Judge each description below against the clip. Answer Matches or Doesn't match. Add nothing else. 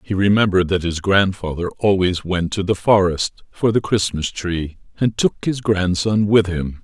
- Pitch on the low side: Matches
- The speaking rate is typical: Matches